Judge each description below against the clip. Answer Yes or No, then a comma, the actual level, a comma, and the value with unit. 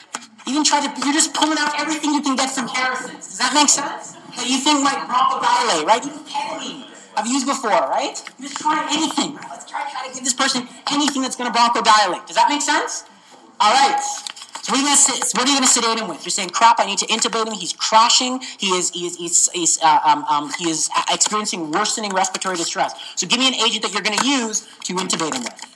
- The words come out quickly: Yes, fast, 240 wpm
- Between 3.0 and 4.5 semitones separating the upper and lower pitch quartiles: No, average, 5.1 semitones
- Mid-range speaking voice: No, very high, 255 Hz